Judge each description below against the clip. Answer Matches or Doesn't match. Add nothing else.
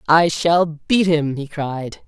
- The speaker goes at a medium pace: Matches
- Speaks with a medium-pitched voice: Matches